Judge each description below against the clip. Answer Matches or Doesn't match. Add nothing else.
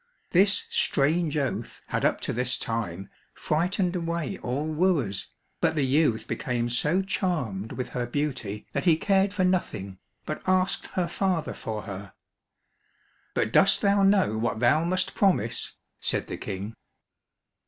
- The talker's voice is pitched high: Doesn't match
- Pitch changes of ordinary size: Doesn't match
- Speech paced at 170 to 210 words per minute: Doesn't match